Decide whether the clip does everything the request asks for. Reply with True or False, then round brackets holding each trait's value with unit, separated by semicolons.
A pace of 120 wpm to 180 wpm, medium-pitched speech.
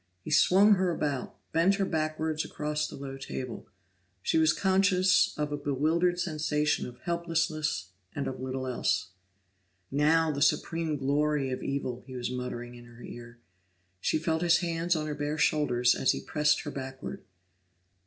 True (165 wpm; 150 Hz)